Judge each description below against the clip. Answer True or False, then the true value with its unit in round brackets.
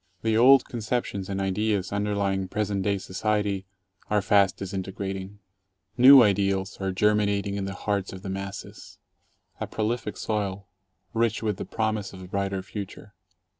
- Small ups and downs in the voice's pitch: True (1.6 semitones)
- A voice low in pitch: True (100 Hz)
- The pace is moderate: True (155 wpm)